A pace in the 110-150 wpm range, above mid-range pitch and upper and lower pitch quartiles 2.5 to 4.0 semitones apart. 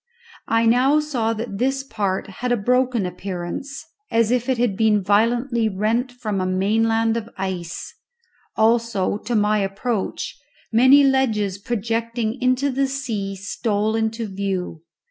Yes: average, 140 wpm; high, 225 Hz; average, 3.4 semitones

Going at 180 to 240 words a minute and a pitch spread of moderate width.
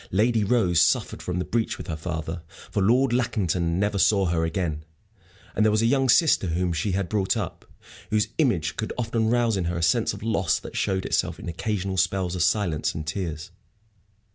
Yes: average, 200 wpm; average, 4.3 semitones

